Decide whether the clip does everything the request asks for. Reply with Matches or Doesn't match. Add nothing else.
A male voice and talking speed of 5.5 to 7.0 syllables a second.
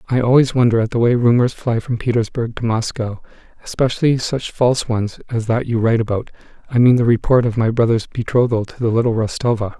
Matches